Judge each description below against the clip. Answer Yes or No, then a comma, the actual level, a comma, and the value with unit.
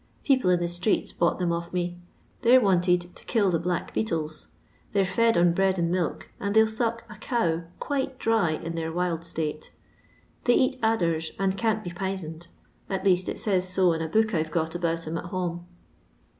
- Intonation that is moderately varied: Yes, average, 4.0 semitones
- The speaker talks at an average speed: No, fast, 210 wpm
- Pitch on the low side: No, medium, 180 Hz